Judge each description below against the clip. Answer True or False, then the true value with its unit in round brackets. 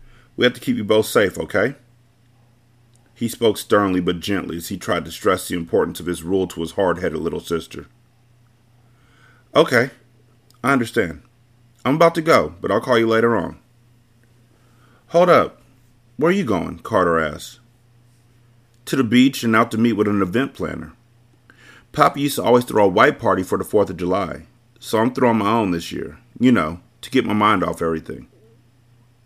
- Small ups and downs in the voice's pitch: True (1.5 semitones)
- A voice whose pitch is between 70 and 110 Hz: False (120 Hz)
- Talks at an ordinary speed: True (185 wpm)